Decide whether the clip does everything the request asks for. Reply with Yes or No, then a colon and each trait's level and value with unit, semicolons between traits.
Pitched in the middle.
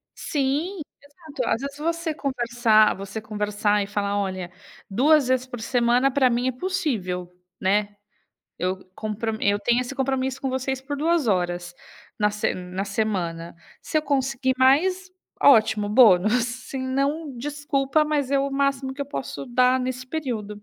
No: very high, 255 Hz